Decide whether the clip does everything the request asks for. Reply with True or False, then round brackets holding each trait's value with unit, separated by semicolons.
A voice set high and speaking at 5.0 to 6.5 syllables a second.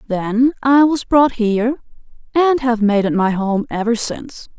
False (240 Hz; 4.5 syllables/s)